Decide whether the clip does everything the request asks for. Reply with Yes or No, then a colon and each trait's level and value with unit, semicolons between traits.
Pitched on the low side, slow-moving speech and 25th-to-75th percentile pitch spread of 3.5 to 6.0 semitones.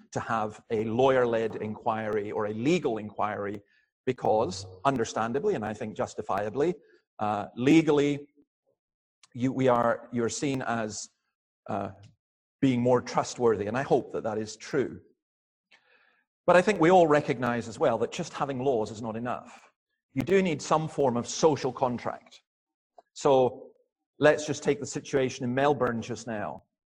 No: low, 125 Hz; average, 145 wpm; average, 4.9 semitones